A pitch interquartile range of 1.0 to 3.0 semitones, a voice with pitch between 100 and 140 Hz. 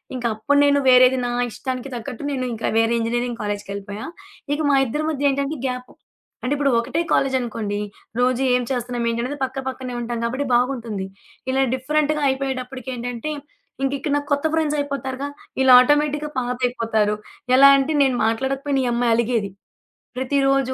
No: narrow, 2.6 semitones; very high, 255 Hz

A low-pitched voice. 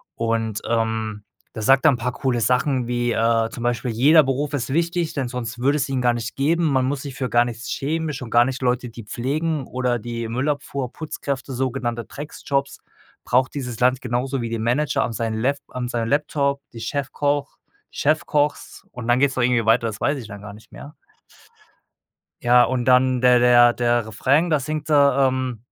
Yes: low, 125 Hz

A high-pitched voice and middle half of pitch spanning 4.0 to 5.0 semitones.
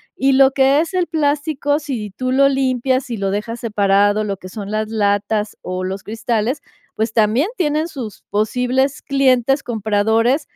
Yes: high, 240 Hz; average, 4.6 semitones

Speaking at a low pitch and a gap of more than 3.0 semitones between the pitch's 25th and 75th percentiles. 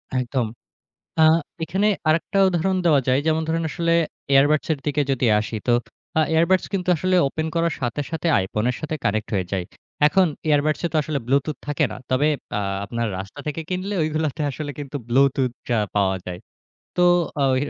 No: medium, 150 Hz; average, 4.2 semitones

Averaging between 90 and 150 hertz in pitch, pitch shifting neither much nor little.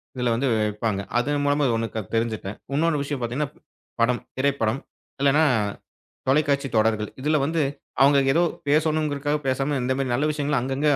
Yes: medium, 140 Hz; average, 3.4 semitones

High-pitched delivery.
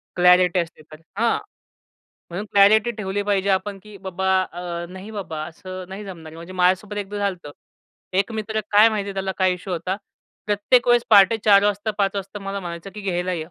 Yes: high, 195 Hz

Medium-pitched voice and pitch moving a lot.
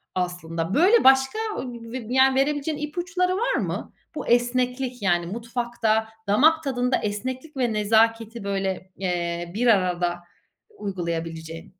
No: high, 230 Hz; wide, 6.0 semitones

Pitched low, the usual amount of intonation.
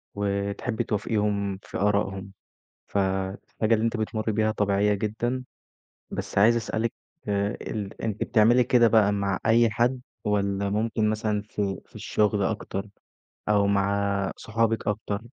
No: low, 105 Hz; narrow, 1.8 semitones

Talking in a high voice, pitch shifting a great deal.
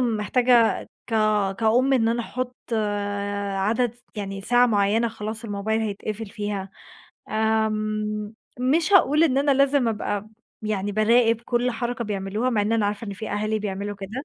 No: high, 220 Hz; average, 2.7 semitones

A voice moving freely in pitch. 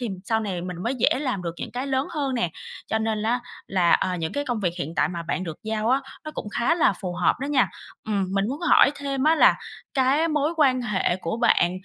Yes: wide, 6.6 semitones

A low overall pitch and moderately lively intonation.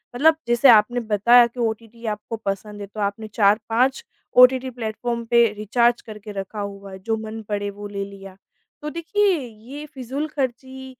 No: high, 225 Hz; average, 3.3 semitones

